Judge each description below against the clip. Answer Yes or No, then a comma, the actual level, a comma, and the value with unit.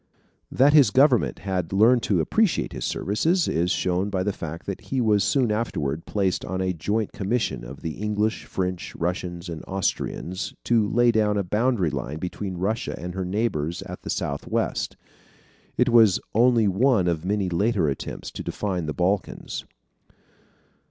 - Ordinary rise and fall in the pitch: Yes, average, 4.2 semitones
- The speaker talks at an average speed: Yes, average, 165 wpm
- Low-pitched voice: Yes, low, 100 Hz